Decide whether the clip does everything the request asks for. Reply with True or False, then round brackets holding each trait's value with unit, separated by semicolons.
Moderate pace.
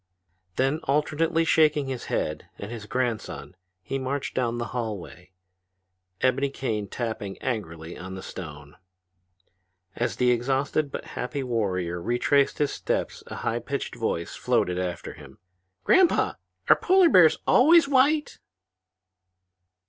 False (125 wpm)